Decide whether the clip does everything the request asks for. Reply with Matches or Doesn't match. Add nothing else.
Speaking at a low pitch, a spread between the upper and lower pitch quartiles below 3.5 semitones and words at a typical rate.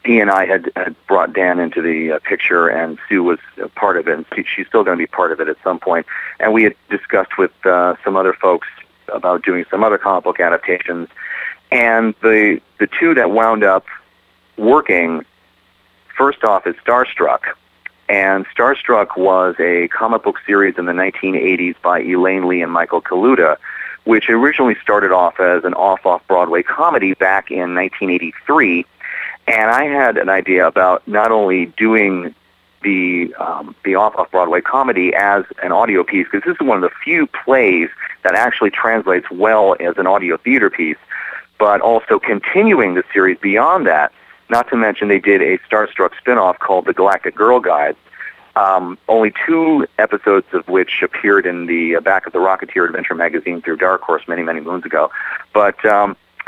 Matches